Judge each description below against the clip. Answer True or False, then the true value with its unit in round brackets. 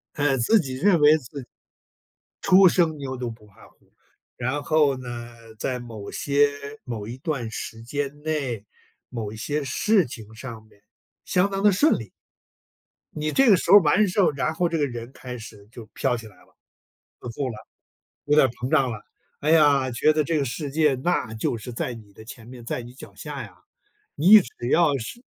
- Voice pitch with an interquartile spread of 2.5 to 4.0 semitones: False (4.8 semitones)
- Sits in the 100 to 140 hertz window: True (135 Hz)